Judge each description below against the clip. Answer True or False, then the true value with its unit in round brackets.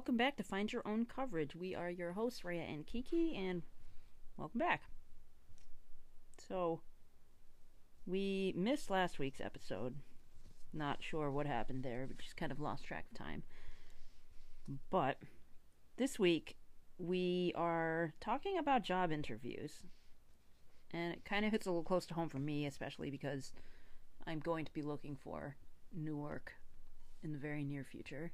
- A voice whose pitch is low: False (150 Hz)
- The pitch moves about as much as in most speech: False (8.2 semitones)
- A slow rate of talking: False (150 wpm)